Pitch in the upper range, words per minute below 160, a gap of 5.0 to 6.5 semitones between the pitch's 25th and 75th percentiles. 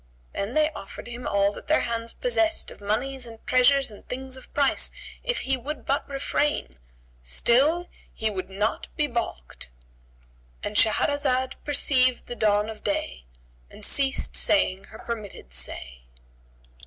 Yes: high, 235 Hz; average, 140 wpm; wide, 5.6 semitones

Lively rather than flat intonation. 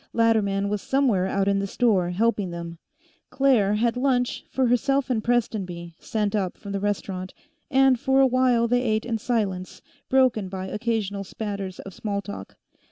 No: average, 3.9 semitones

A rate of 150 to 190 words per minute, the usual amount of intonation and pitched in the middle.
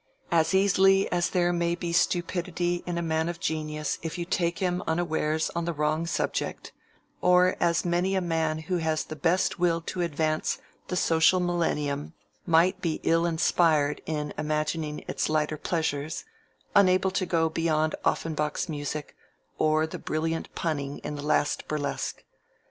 No: average, 155 wpm; narrow, 2.1 semitones; medium, 165 Hz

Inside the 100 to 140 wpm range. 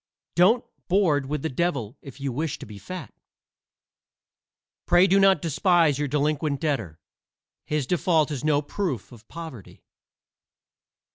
Yes: slow, 135 wpm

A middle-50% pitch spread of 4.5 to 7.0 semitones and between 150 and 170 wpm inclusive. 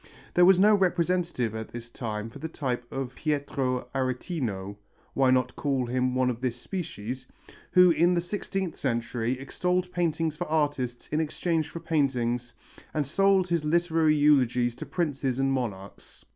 Yes: average, 5.3 semitones; average, 160 wpm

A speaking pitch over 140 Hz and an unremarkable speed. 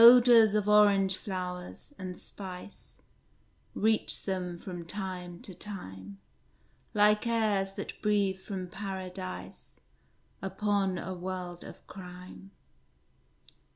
No: high, 190 Hz; slow, 100 wpm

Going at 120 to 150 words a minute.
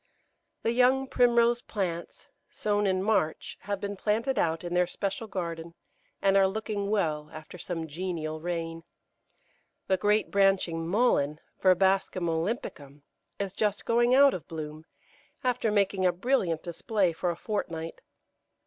Yes: average, 140 wpm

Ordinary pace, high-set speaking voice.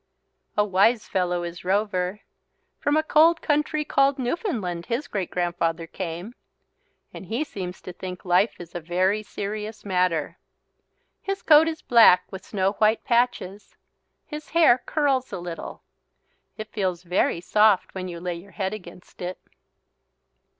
Yes: average, 145 wpm; high, 195 Hz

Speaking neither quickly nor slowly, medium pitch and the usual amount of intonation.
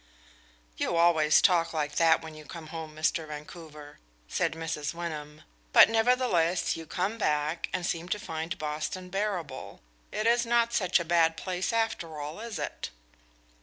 Yes: average, 160 wpm; medium, 165 Hz; average, 3.4 semitones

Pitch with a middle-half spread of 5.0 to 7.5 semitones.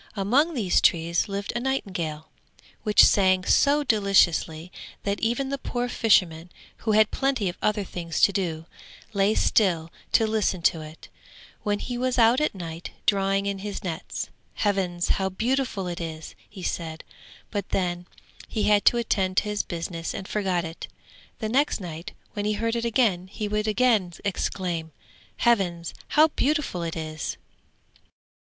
No: average, 4.4 semitones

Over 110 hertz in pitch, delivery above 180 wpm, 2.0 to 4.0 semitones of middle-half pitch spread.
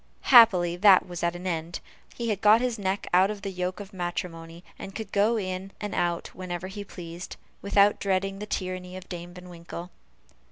Yes: medium, 185 Hz; average, 195 wpm; narrow, 2.4 semitones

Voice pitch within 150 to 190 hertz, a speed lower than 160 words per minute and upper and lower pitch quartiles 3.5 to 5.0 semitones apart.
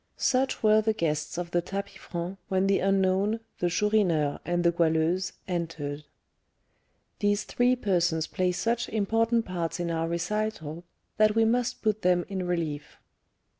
Yes: medium, 185 Hz; average, 150 wpm; average, 4.0 semitones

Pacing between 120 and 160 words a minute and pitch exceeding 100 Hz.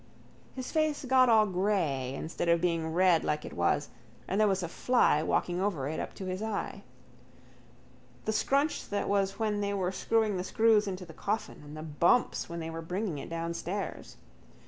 No: average, 190 wpm; medium, 185 Hz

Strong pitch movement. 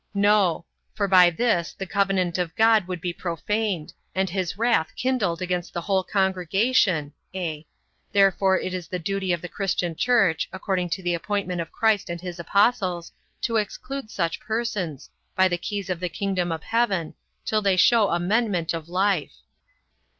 No: average, 3.0 semitones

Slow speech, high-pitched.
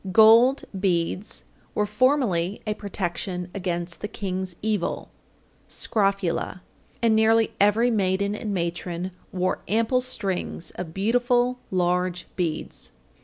Yes: slow, 110 wpm; high, 200 Hz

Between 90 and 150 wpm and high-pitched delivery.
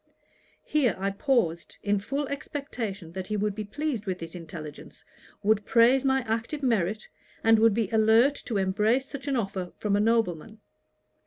No: average, 165 wpm; high, 220 Hz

